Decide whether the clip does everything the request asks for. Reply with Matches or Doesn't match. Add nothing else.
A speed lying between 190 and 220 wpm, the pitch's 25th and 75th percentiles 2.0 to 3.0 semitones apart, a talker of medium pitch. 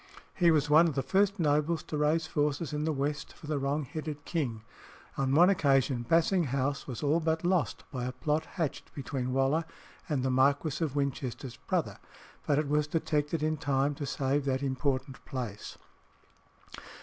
Doesn't match